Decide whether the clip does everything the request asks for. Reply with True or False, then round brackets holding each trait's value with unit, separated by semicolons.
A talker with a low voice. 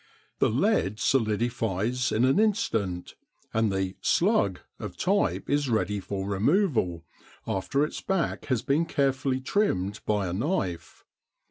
True (115 Hz)